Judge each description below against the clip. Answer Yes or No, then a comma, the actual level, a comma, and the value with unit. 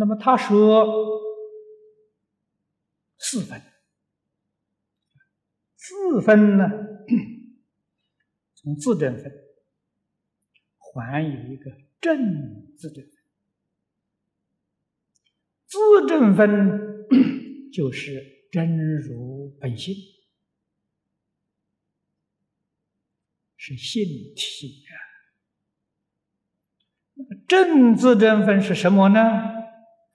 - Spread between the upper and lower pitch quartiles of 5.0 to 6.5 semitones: No, wide, 8.8 semitones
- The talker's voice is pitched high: Yes, high, 210 Hz